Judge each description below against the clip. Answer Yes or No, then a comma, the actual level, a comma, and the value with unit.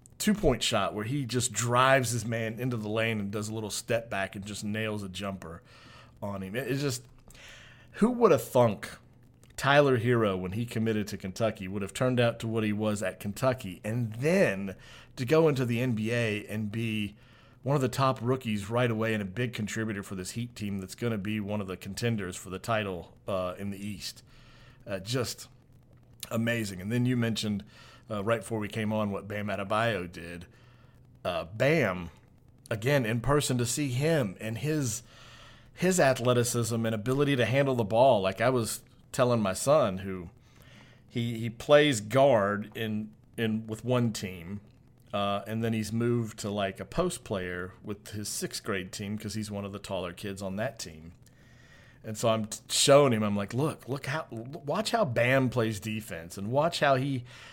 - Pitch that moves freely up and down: No, average, 3.2 semitones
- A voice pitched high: No, low, 115 Hz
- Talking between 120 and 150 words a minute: No, average, 190 wpm